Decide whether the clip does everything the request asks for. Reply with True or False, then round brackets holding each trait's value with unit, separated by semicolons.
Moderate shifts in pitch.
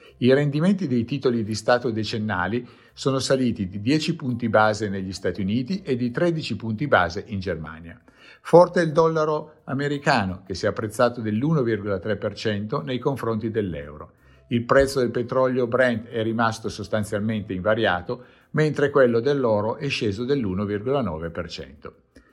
True (4.6 semitones)